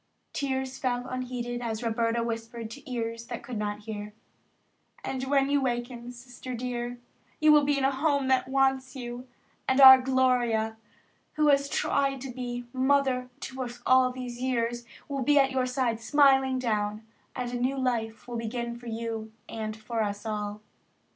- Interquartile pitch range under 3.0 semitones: Yes, narrow, 2.4 semitones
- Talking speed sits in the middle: Yes, average, 170 wpm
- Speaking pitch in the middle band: No, very high, 250 Hz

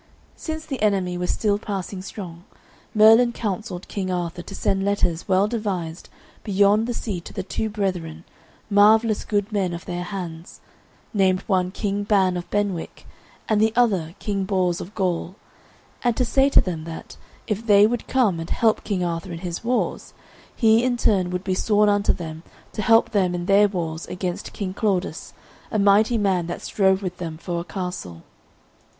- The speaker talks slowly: No, average, 180 wpm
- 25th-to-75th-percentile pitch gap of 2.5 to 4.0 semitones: Yes, average, 3.1 semitones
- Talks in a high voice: Yes, high, 195 Hz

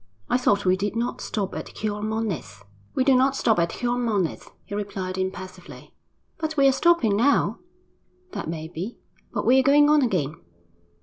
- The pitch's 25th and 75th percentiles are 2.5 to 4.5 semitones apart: No, wide, 5.5 semitones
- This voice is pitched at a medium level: No, high, 215 Hz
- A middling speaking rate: Yes, average, 170 wpm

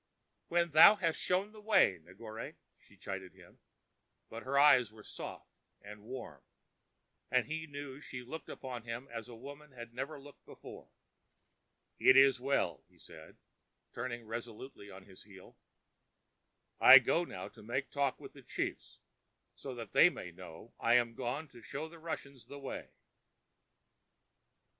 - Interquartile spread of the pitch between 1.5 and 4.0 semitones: No, average, 4.4 semitones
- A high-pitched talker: No, low, 125 Hz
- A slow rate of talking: No, average, 150 wpm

